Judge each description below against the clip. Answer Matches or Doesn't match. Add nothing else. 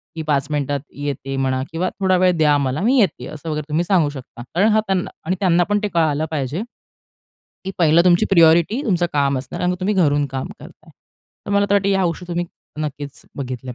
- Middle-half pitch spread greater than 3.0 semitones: Matches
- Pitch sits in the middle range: Matches